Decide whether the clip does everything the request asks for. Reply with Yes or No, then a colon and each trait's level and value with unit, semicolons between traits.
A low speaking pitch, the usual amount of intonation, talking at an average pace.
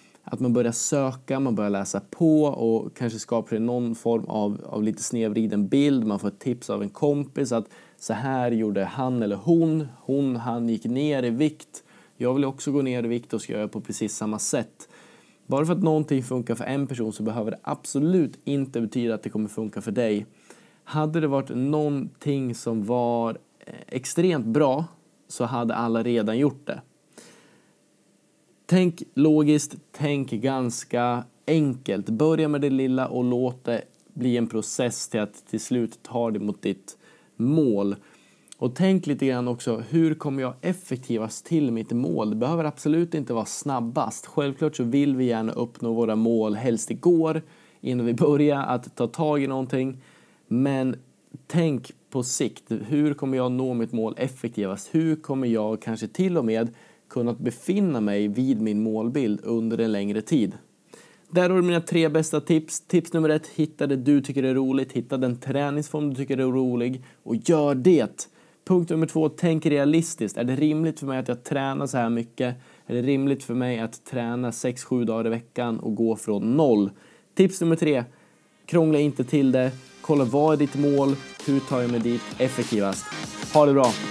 Yes: low, 130 Hz; average, 4.3 semitones; average, 180 wpm